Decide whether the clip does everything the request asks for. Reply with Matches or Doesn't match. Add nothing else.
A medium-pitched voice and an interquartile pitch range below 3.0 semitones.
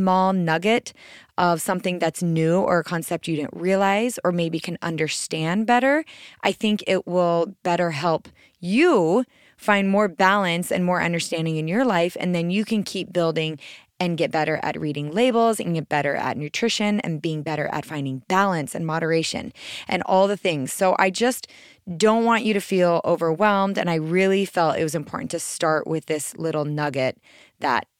Doesn't match